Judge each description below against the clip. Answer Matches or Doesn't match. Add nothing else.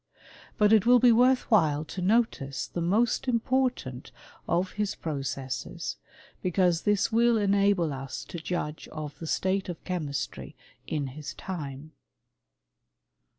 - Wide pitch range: Matches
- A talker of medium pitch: Matches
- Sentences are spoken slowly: Matches